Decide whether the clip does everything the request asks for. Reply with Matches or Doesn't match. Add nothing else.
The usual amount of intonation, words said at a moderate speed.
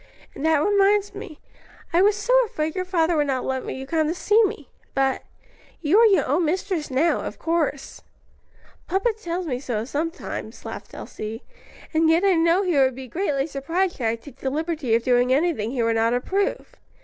Doesn't match